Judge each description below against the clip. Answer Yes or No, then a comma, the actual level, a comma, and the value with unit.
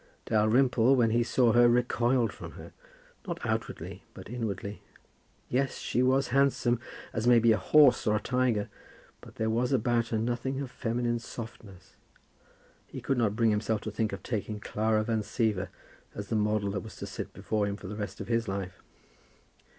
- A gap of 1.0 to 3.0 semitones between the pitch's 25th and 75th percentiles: Yes, narrow, 2.4 semitones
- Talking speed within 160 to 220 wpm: Yes, average, 180 wpm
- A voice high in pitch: No, low, 115 Hz